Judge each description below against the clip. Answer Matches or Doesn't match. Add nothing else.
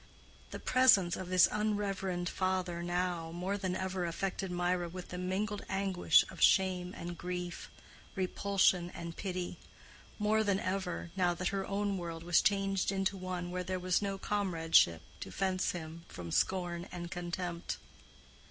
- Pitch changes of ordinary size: Doesn't match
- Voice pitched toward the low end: Doesn't match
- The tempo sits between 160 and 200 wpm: Doesn't match